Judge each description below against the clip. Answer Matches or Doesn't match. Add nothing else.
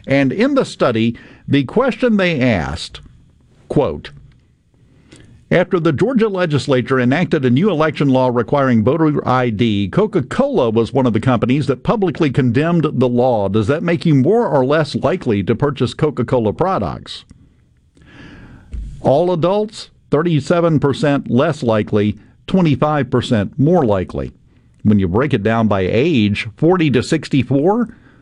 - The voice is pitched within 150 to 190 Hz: Doesn't match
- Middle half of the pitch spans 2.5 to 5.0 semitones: Doesn't match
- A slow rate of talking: Matches